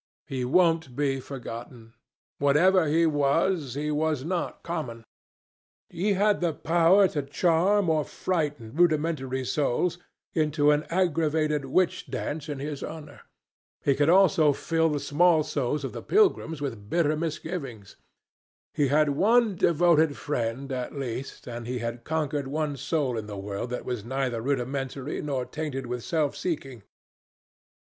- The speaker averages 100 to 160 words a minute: Yes, average, 145 wpm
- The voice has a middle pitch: Yes, medium, 145 Hz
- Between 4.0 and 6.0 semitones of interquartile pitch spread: No, average, 3.6 semitones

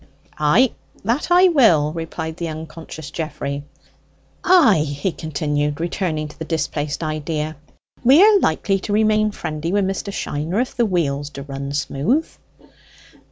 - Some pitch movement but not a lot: No, wide, 5.9 semitones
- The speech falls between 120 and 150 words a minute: Yes, slow, 135 wpm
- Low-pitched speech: No, medium, 160 Hz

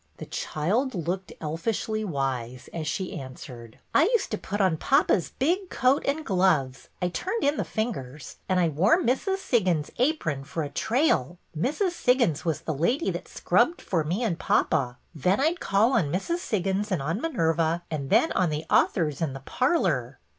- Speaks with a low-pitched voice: No, medium, 185 Hz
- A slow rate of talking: No, average, 185 wpm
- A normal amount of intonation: No, wide, 8.7 semitones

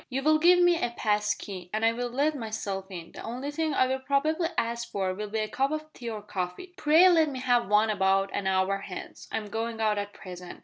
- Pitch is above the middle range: Yes, high, 225 Hz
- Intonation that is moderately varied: No, wide, 5.8 semitones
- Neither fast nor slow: No, fast, 245 wpm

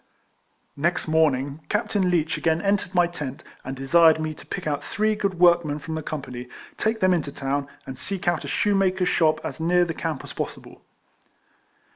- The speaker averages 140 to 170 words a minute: No, average, 195 wpm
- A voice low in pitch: No, medium, 165 Hz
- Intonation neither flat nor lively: Yes, average, 3.9 semitones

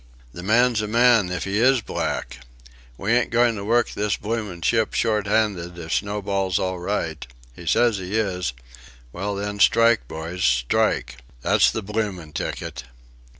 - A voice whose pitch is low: Yes, low, 100 Hz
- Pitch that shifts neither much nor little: Yes, average, 3.9 semitones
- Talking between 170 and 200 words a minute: No, average, 150 wpm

